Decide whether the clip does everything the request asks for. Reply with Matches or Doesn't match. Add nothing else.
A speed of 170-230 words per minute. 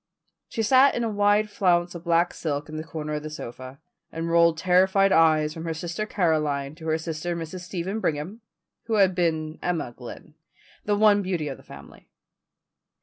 Matches